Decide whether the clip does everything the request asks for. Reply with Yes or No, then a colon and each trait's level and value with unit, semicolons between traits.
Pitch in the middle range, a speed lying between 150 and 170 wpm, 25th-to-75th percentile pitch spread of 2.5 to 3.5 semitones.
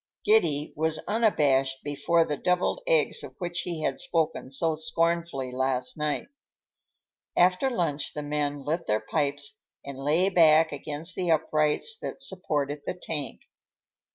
No: medium, 155 Hz; average, 140 wpm; average, 3.2 semitones